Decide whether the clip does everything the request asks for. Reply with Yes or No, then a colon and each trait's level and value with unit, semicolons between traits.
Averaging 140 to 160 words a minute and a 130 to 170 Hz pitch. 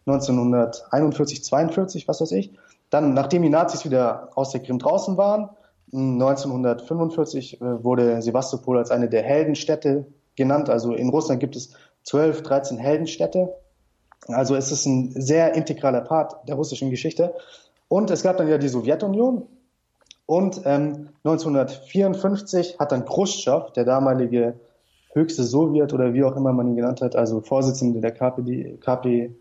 Yes: average, 145 wpm; medium, 140 Hz